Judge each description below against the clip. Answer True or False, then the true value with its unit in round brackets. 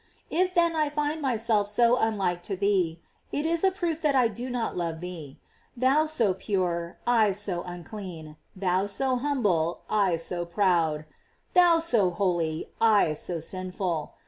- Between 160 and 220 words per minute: True (165 wpm)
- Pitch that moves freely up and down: True (6.8 semitones)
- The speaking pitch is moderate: False (205 Hz)